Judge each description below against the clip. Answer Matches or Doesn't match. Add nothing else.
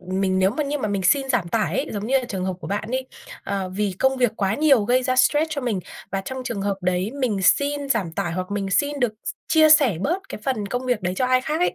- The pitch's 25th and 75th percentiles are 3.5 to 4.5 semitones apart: Doesn't match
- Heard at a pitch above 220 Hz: Matches